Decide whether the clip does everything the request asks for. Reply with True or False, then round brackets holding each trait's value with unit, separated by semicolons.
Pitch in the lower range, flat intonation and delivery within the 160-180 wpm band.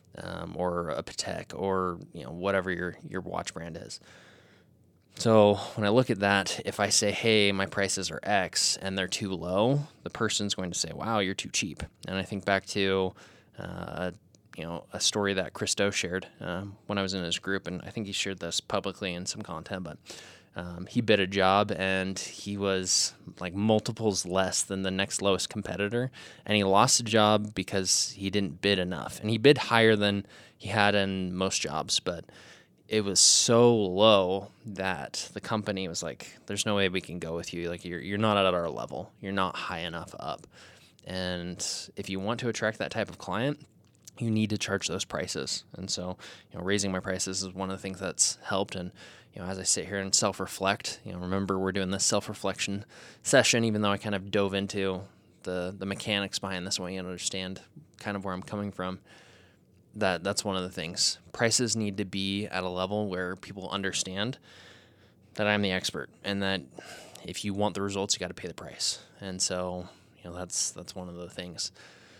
False (95 Hz; 2.0 semitones; 205 wpm)